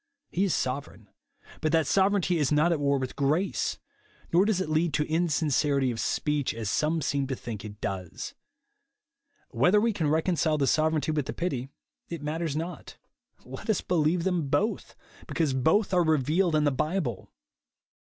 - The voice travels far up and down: No, average, 3.8 semitones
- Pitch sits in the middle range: Yes, medium, 155 Hz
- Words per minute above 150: Yes, average, 170 wpm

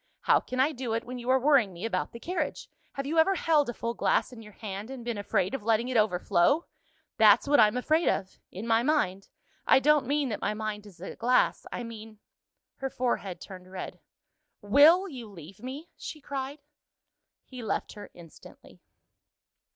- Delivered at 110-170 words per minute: No, average, 195 wpm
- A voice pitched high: Yes, high, 240 Hz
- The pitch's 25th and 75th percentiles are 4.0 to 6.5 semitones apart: Yes, average, 5.1 semitones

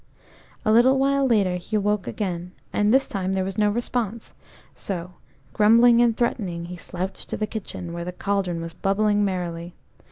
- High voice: Yes, high, 200 Hz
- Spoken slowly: No, average, 170 wpm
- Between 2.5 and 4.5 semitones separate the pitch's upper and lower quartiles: Yes, average, 3.7 semitones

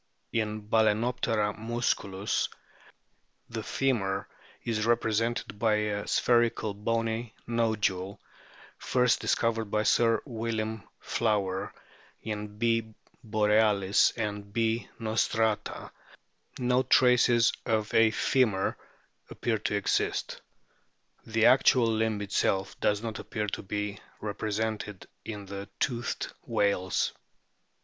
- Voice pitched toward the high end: No, low, 110 Hz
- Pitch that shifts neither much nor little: No, narrow, 1.9 semitones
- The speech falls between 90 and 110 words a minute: Yes, slow, 100 wpm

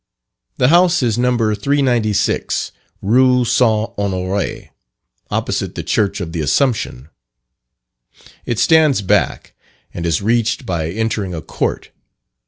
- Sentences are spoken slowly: Yes, slow, 115 wpm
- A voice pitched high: No, low, 110 Hz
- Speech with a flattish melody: No, average, 4.4 semitones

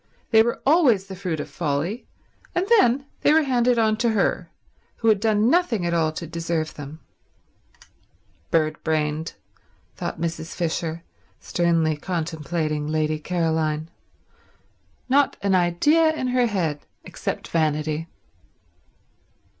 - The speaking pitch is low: No, medium, 170 Hz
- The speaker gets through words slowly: Yes, slow, 125 wpm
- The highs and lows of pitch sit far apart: Yes, wide, 6.3 semitones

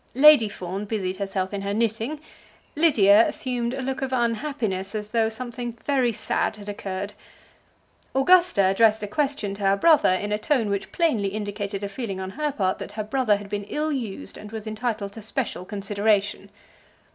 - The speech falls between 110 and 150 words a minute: No, average, 180 wpm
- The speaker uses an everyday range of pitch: Yes, average, 4.0 semitones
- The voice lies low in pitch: No, high, 215 Hz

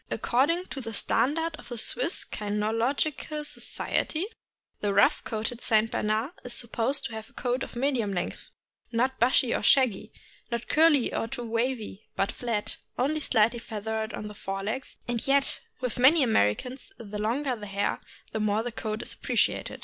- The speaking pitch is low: No, high, 235 Hz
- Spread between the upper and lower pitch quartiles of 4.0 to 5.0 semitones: No, average, 3.6 semitones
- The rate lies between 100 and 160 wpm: No, average, 170 wpm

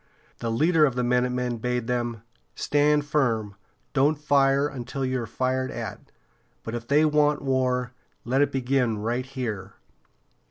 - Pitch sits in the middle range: No, low, 130 Hz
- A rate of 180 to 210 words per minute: No, average, 150 wpm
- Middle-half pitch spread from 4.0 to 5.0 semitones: No, average, 2.8 semitones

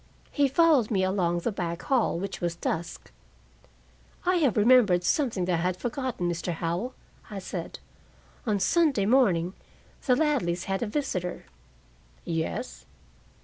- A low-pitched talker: No, high, 195 Hz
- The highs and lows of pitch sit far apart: Yes, wide, 6.6 semitones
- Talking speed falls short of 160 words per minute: Yes, average, 140 wpm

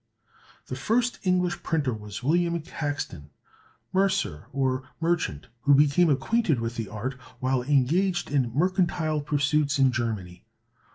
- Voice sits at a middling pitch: Yes, medium, 145 Hz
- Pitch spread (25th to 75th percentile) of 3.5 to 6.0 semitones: Yes, wide, 5.6 semitones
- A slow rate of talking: Yes, slow, 125 wpm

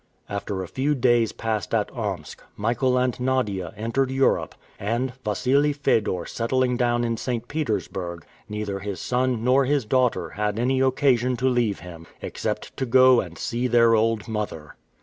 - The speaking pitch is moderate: No, low, 120 Hz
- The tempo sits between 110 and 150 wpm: No, average, 160 wpm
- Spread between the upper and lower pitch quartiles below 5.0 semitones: Yes, average, 3.5 semitones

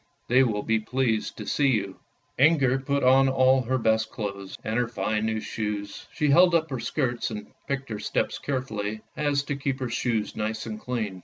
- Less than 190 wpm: No, fast, 205 wpm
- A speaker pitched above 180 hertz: No, low, 120 Hz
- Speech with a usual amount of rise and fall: Yes, average, 3.8 semitones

